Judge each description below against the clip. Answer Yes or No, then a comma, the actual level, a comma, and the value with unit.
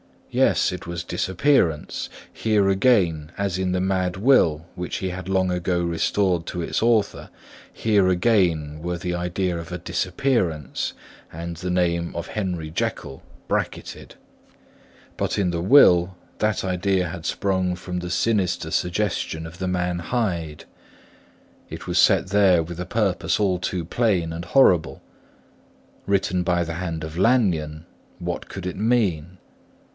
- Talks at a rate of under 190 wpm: Yes, average, 145 wpm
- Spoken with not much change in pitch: Yes, narrow, 2.3 semitones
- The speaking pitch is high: No, very low, 90 Hz